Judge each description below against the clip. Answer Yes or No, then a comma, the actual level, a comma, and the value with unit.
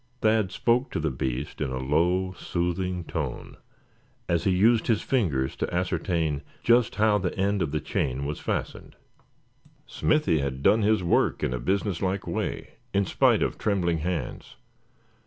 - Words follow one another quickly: No, average, 160 wpm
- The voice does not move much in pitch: No, average, 5.2 semitones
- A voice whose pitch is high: No, very low, 90 Hz